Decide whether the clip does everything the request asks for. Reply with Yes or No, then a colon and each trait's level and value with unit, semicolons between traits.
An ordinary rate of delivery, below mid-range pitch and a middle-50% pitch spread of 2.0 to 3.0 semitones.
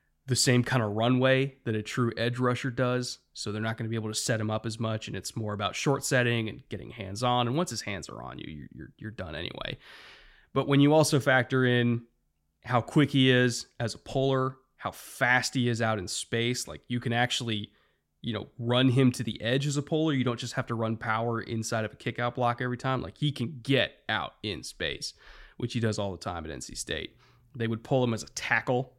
No: fast, 240 wpm; low, 120 Hz; narrow, 2.6 semitones